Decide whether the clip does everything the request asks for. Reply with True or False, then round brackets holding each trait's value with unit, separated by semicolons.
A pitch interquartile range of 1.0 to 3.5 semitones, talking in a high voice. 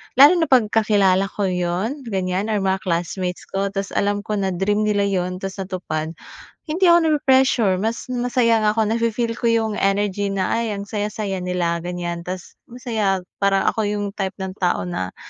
True (3.2 semitones; 200 Hz)